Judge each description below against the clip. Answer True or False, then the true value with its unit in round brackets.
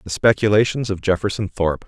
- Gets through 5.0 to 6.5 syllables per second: True (6.2 syllables/s)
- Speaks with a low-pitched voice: True (95 Hz)